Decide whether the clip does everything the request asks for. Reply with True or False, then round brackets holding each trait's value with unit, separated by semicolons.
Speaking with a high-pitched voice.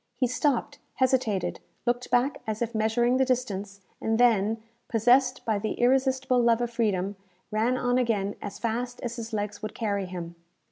True (235 Hz)